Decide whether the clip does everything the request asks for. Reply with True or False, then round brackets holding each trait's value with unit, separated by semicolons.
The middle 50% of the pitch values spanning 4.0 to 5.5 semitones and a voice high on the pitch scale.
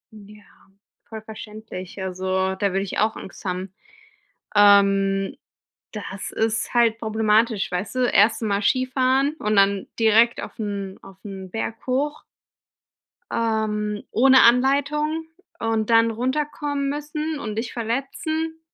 True (4.3 semitones; 220 Hz)